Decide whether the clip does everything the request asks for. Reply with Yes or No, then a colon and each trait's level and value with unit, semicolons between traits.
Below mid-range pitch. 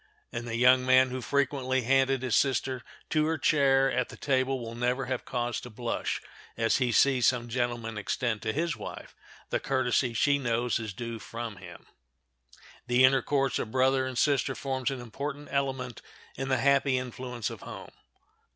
Yes: low, 130 Hz